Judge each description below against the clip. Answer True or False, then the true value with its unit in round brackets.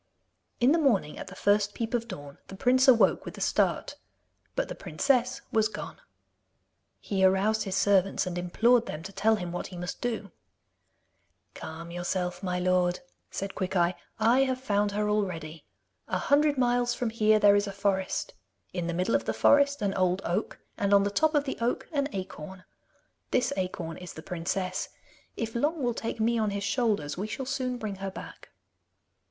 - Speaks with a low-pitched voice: False (205 Hz)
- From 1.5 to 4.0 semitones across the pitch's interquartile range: False (4.7 semitones)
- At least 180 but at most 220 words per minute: True (185 wpm)